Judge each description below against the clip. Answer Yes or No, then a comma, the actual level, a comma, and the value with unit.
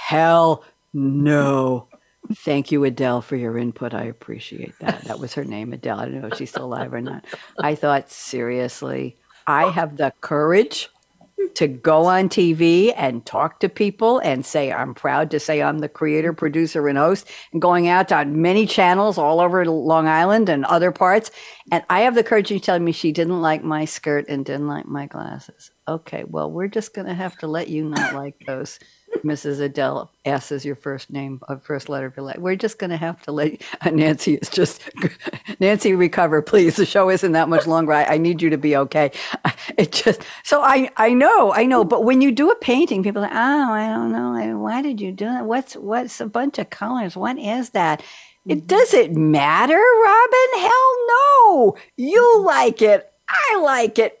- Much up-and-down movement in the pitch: Yes, wide, 7.0 semitones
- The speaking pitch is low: No, medium, 165 Hz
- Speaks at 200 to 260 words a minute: Yes, fast, 205 wpm